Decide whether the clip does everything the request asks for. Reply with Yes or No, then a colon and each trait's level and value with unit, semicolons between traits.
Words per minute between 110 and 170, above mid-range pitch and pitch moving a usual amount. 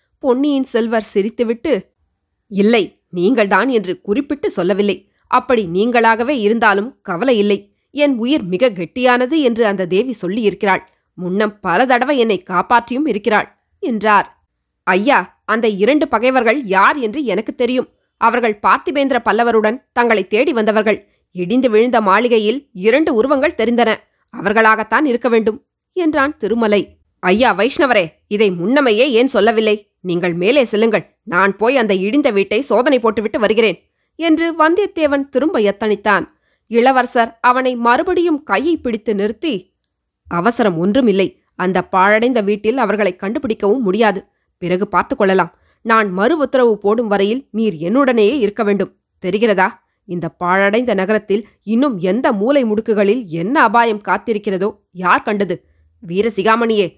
Yes: average, 120 wpm; high, 220 Hz; average, 3.7 semitones